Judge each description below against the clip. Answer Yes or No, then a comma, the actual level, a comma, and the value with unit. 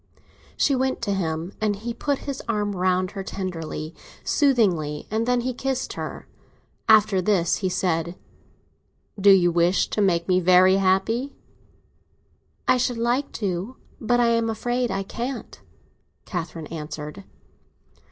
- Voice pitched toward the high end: Yes, high, 195 Hz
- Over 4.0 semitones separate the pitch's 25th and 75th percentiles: Yes, average, 5.1 semitones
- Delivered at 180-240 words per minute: No, slow, 135 wpm